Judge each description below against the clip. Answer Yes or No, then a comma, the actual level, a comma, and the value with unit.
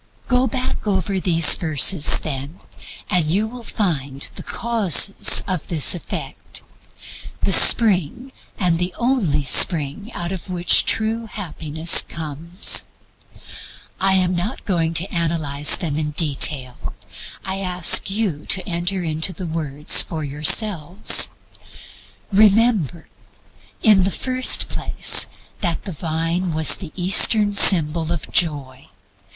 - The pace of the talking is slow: Yes, slow, 125 wpm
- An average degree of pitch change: Yes, average, 4.1 semitones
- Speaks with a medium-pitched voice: Yes, medium, 175 Hz